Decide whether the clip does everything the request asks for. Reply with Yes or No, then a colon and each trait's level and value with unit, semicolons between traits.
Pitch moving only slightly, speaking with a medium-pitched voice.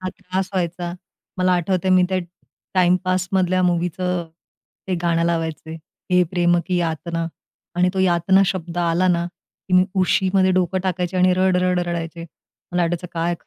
Yes: narrow, 1.3 semitones; medium, 180 Hz